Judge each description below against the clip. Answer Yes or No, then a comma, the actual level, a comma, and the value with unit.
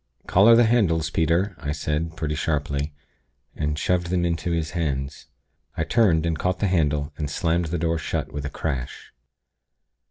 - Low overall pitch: Yes, very low, 80 Hz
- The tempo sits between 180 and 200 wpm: No, average, 165 wpm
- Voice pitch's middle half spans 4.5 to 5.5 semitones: No, average, 2.7 semitones